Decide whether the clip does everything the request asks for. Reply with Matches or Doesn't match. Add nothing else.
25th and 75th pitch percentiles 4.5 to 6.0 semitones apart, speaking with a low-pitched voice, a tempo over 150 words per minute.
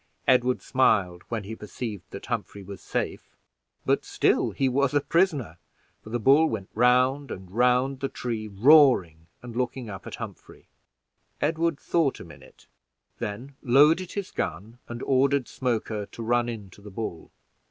Matches